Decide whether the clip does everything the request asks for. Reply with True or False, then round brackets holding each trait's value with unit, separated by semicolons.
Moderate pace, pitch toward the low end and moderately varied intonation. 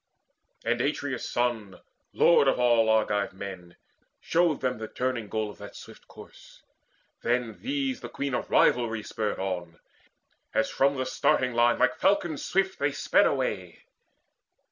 True (145 wpm; 120 Hz; 4.6 semitones)